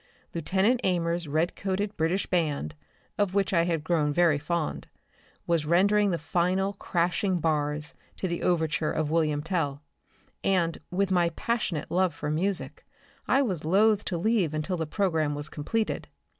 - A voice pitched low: No, medium, 170 Hz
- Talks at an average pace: Yes, average, 150 wpm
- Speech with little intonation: No, average, 3.6 semitones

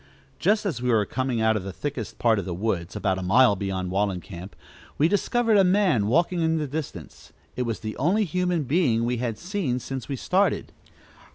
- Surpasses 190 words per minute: Yes, average, 200 wpm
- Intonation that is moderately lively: No, wide, 8.5 semitones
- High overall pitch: No, low, 125 Hz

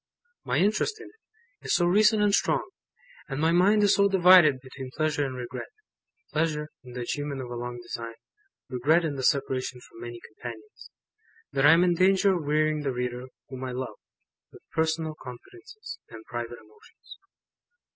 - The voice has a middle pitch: Yes, medium, 145 Hz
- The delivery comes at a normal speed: Yes, average, 175 wpm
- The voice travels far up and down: Yes, wide, 6.3 semitones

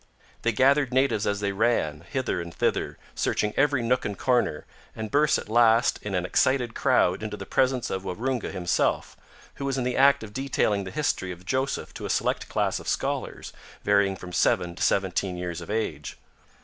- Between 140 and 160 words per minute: No, average, 190 wpm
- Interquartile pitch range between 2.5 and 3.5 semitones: No, wide, 5.4 semitones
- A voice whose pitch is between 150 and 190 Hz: No, low, 110 Hz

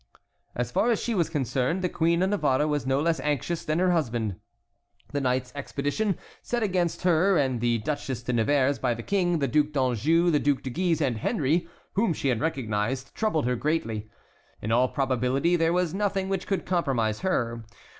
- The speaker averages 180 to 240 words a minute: Yes, average, 190 wpm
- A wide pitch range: Yes, wide, 5.7 semitones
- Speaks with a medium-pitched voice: Yes, medium, 145 Hz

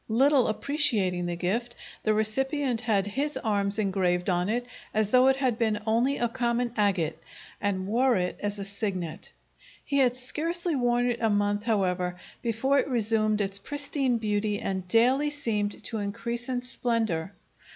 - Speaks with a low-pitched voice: No, high, 220 Hz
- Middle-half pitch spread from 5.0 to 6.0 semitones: No, average, 3.8 semitones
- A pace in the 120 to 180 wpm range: Yes, average, 160 wpm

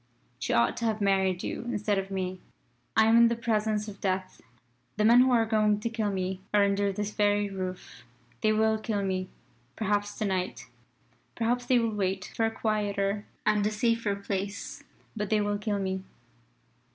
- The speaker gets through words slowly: No, average, 185 wpm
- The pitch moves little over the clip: Yes, narrow, 2.0 semitones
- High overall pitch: Yes, high, 205 Hz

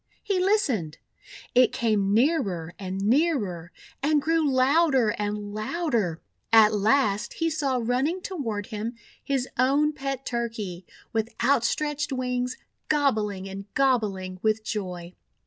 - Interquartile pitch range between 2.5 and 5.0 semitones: No, wide, 5.5 semitones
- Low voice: No, high, 235 Hz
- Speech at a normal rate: No, slow, 125 wpm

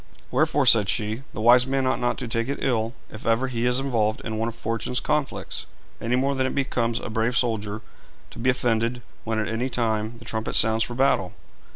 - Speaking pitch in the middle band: No, low, 115 Hz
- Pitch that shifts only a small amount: Yes, narrow, 2.2 semitones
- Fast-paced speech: Yes, fast, 215 wpm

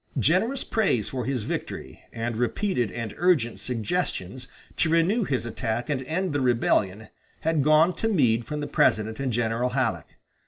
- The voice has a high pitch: No, low, 130 Hz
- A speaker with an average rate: Yes, average, 160 wpm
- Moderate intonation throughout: No, wide, 6.1 semitones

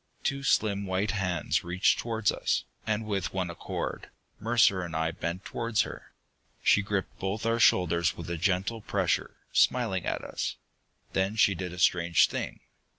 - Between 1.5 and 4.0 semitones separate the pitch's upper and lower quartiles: Yes, average, 3.4 semitones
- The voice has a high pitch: No, very low, 95 Hz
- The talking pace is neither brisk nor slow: Yes, average, 160 wpm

